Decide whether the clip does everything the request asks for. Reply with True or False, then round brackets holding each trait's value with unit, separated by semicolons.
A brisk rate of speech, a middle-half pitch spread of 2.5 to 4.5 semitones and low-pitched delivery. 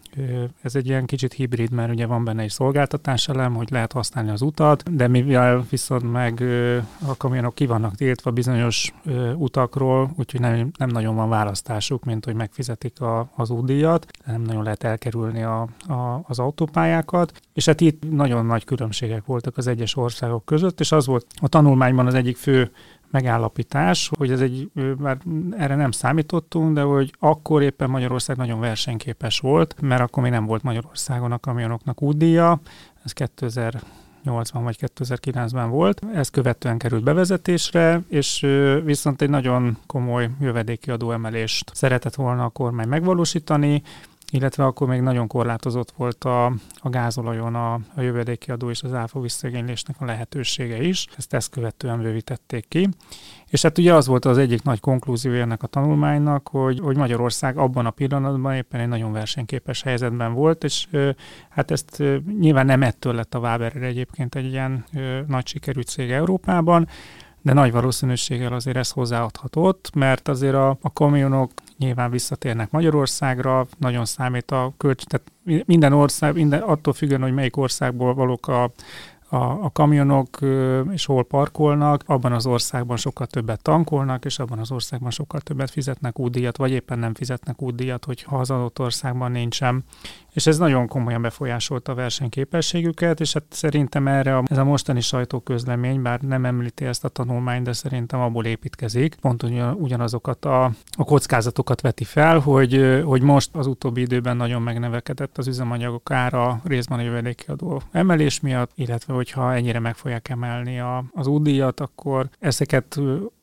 True (160 wpm; 2.8 semitones; 130 Hz)